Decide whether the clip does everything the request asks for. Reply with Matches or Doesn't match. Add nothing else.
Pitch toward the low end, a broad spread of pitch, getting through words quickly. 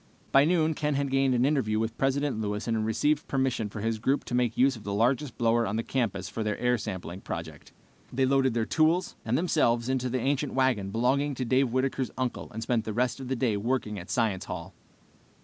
Doesn't match